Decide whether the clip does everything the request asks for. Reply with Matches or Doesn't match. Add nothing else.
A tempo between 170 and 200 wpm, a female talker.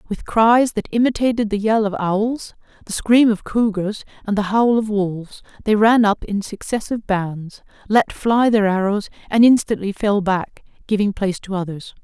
Matches